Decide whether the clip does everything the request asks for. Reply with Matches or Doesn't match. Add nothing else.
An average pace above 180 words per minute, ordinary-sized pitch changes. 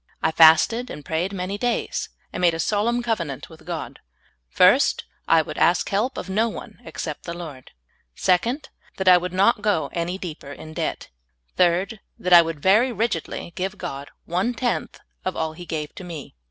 Matches